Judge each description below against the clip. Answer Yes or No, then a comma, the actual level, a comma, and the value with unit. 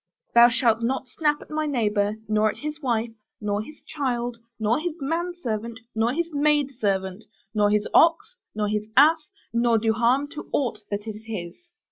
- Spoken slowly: No, average, 170 wpm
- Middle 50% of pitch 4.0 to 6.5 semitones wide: Yes, wide, 5.6 semitones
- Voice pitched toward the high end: Yes, high, 235 Hz